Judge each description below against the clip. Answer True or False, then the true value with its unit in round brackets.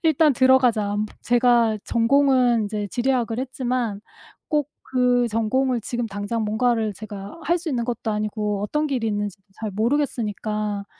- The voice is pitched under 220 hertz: False (235 Hz)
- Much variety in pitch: False (3.4 semitones)